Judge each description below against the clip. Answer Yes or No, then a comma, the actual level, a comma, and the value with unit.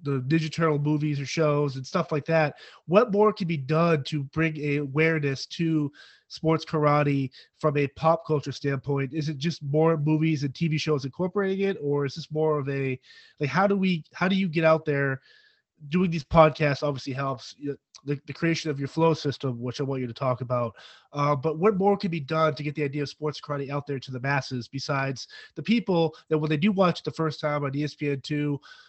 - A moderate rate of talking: No, fast, 220 wpm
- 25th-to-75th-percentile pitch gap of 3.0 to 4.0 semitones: No, narrow, 2.4 semitones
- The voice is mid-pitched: Yes, medium, 150 Hz